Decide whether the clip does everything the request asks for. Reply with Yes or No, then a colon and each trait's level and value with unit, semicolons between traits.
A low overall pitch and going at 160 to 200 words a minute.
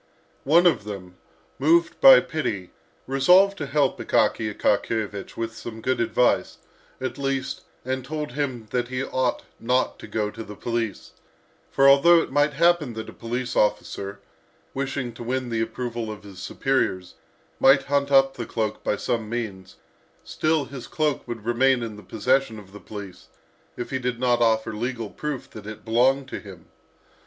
Yes: low, 120 Hz; average, 170 wpm